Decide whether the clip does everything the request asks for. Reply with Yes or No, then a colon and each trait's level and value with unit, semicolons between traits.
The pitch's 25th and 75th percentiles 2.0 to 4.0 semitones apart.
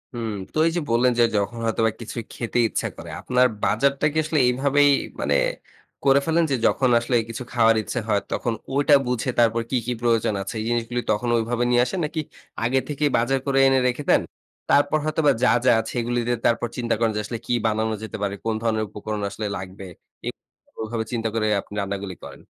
Yes: average, 3.1 semitones